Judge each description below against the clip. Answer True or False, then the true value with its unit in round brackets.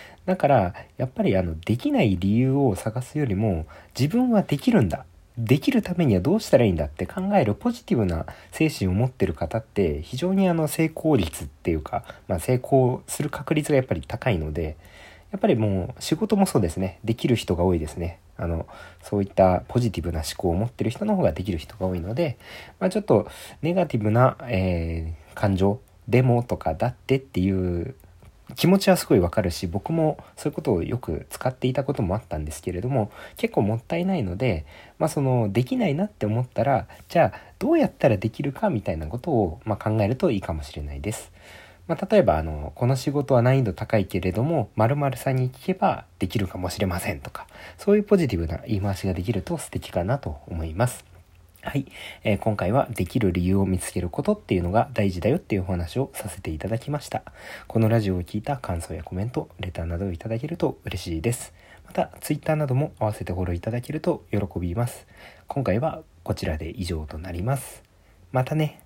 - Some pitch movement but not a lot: False (6.8 semitones)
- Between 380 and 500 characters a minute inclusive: True (410 characters per minute)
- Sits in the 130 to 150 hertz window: False (110 Hz)